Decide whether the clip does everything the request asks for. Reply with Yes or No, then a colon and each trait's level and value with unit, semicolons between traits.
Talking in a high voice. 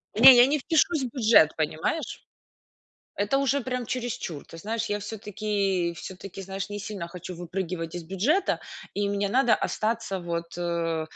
Yes: high, 200 Hz